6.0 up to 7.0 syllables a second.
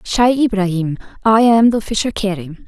No: 4.8 syllables/s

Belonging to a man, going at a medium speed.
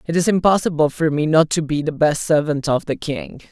No: male; fast, 240 wpm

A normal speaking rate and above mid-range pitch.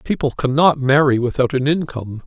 No: average, 160 wpm; medium, 140 Hz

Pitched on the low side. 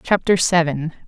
No: medium, 170 Hz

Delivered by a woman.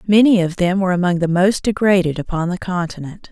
Yes: female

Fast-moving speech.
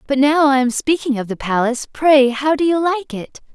Yes: fast, 235 wpm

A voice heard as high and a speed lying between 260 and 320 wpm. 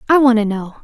Yes: high, 235 Hz; fast, 290 wpm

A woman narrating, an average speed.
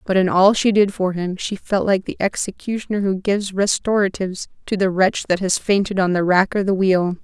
No: female; fast, 225 wpm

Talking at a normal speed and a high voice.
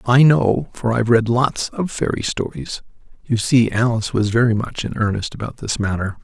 No: average, 195 wpm; low, 115 Hz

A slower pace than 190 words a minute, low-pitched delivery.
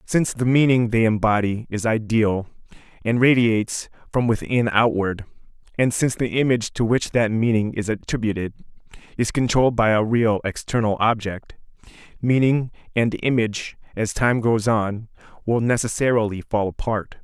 Yes: average, 140 wpm; low, 115 Hz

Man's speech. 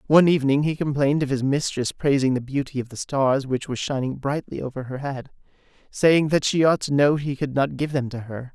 Yes: male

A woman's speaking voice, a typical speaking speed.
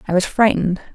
Yes: female; average, 190 wpm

